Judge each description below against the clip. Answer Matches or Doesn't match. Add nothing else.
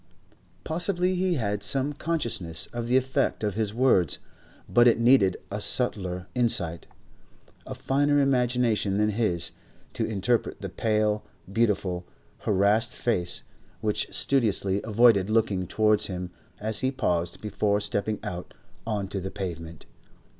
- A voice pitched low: Matches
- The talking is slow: Matches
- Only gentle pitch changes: Doesn't match